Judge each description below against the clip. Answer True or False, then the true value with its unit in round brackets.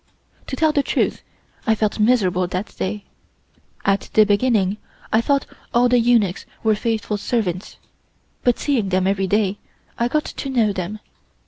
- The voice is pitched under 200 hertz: False (215 Hz)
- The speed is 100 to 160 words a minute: True (155 wpm)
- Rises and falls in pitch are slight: False (4.0 semitones)